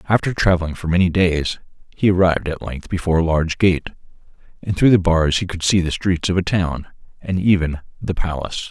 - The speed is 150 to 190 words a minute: No, average, 200 wpm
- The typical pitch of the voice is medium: No, very low, 85 Hz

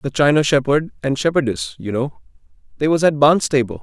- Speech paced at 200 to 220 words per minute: No, average, 170 wpm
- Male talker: Yes, male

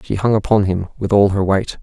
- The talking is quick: Yes, fast, 265 wpm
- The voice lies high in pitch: No, low, 100 Hz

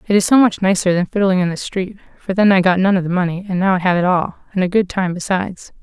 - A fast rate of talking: Yes, fast, 300 wpm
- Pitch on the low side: No, medium, 185 Hz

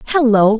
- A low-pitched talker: No, high, 235 Hz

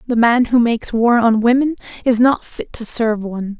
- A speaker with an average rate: No, fast, 215 wpm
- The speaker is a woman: Yes, female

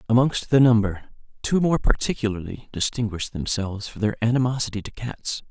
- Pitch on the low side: Yes, low, 115 Hz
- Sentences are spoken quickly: No, average, 140 wpm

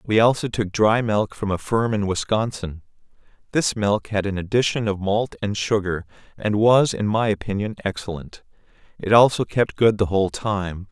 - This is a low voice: Yes, low, 105 Hz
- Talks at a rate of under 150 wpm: No, average, 175 wpm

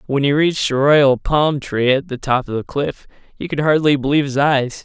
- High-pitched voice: No, medium, 140 Hz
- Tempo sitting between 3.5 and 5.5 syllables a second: Yes, 5.2 syllables/s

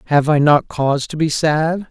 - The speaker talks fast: Yes, fast, 220 wpm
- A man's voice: Yes, male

